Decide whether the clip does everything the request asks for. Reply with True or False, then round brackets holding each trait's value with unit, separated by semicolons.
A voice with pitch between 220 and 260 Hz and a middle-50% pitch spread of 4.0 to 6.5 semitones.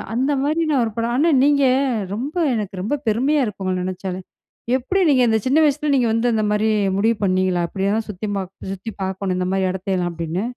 False (210 Hz; 5.5 semitones)